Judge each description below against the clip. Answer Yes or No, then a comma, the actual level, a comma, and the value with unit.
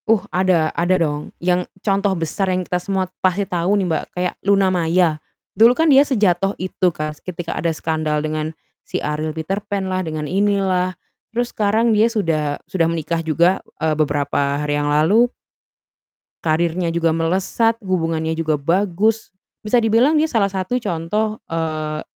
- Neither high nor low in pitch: Yes, medium, 180 Hz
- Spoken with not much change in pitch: No, average, 4.0 semitones